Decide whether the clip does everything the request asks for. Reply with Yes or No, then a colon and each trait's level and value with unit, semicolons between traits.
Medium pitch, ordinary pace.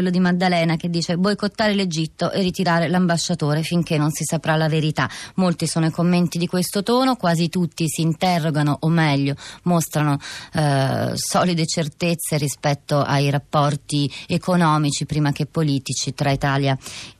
Yes: medium, 160 Hz; average, 155 wpm